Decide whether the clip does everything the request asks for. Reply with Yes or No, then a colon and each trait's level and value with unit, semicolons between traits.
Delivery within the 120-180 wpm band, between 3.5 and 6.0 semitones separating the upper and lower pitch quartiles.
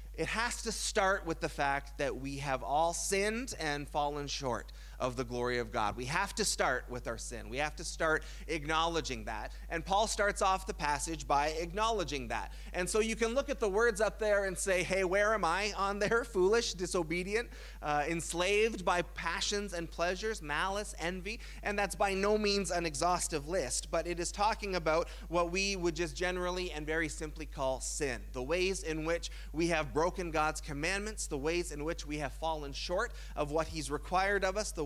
No: average, 200 wpm; average, 4.7 semitones